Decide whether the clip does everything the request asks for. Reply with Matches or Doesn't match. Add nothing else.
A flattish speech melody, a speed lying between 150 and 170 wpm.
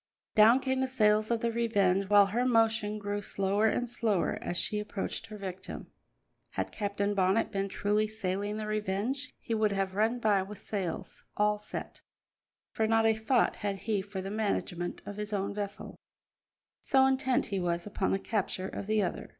Doesn't match